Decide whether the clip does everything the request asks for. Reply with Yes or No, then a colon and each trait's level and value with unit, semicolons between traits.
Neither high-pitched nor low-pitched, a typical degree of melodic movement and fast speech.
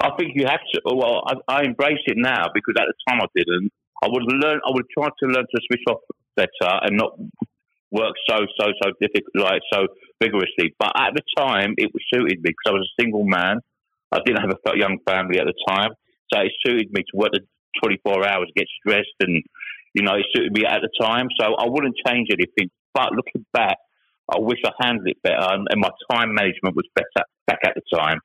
No: low, 130 Hz; average, 3.6 semitones; fast, 225 wpm